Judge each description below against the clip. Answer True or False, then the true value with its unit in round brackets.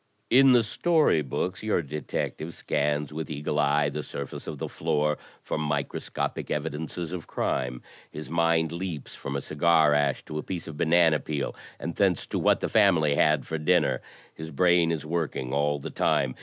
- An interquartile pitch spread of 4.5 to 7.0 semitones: False (2.4 semitones)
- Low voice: True (75 Hz)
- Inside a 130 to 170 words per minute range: False (185 wpm)